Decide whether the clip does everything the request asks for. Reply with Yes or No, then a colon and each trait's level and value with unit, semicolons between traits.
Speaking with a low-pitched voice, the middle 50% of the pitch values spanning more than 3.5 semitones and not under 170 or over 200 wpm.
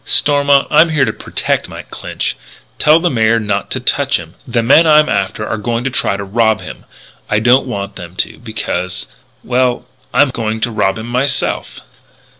Yes: low, 115 Hz; average, 4.1 semitones; average, 185 wpm